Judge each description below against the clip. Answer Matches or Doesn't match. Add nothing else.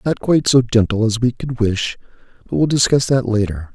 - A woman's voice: Doesn't match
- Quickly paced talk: Matches